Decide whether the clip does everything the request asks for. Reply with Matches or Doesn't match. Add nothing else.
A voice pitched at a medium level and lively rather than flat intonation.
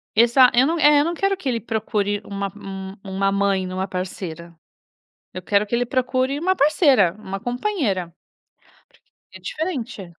Doesn't match